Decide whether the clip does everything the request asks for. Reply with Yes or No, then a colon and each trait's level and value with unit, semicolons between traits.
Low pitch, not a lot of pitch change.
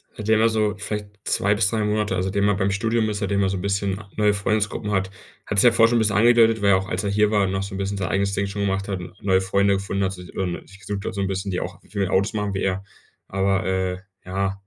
Yes: low, 100 Hz; narrow, 1.4 semitones